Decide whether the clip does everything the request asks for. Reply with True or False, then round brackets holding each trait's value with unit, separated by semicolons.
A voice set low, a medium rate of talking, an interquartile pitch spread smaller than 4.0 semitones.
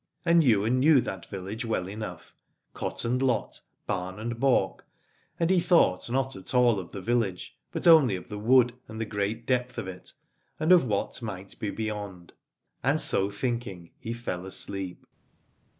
False (110 Hz; 170 wpm; 4.5 semitones)